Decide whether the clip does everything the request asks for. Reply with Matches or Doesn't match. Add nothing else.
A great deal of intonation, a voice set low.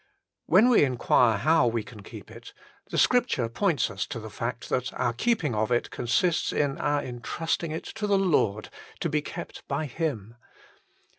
Matches